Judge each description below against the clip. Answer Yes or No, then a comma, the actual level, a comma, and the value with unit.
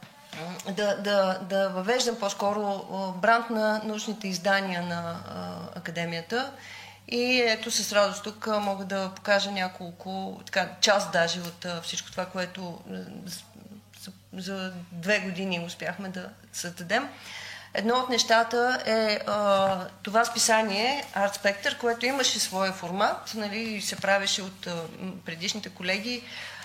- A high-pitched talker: Yes, high, 195 Hz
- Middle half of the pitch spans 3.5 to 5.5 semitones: No, average, 3.1 semitones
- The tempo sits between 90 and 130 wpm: Yes, average, 125 wpm